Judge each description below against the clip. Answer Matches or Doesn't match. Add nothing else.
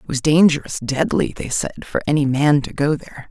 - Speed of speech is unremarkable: Doesn't match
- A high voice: Doesn't match